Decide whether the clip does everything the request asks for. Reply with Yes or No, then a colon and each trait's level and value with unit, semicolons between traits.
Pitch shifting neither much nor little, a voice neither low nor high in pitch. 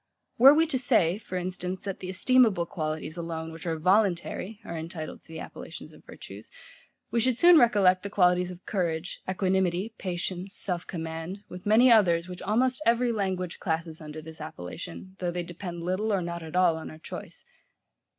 Yes: average, 3.4 semitones; medium, 180 Hz